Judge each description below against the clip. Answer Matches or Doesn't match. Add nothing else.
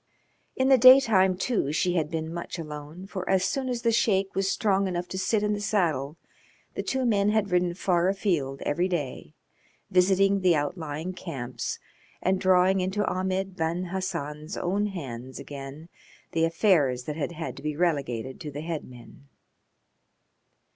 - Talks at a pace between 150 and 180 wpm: Matches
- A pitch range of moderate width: Matches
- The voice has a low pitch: Doesn't match